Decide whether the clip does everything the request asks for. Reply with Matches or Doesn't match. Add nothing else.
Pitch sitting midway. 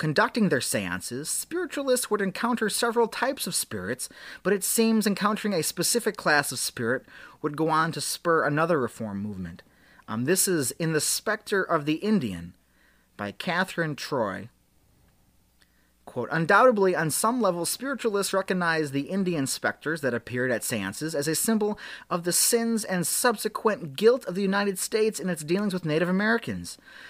Matches